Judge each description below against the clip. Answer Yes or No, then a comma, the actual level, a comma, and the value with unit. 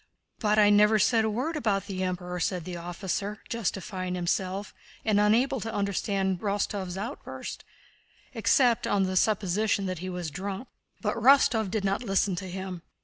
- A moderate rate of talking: Yes, average, 160 wpm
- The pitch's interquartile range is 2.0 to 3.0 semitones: Yes, average, 2.7 semitones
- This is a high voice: Yes, high, 200 Hz